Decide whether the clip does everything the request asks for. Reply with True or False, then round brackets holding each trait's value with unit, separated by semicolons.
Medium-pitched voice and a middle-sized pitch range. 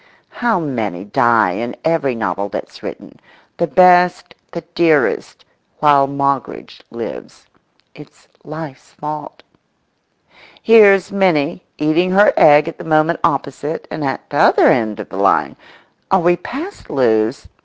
True (150 Hz; 4.9 semitones)